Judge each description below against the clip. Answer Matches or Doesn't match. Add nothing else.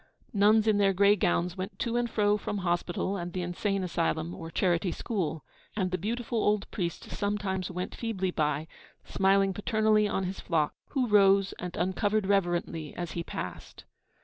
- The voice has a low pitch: Doesn't match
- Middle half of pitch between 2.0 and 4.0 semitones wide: Matches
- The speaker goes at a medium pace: Matches